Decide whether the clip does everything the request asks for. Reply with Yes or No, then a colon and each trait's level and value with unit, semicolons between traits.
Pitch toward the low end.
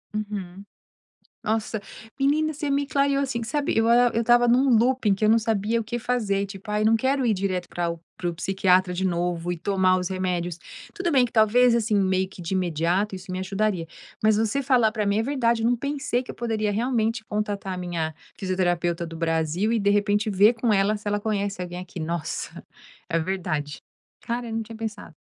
No: high, 210 Hz